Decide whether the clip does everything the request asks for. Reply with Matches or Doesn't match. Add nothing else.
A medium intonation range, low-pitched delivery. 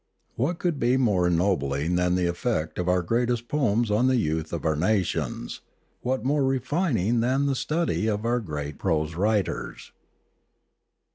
Doesn't match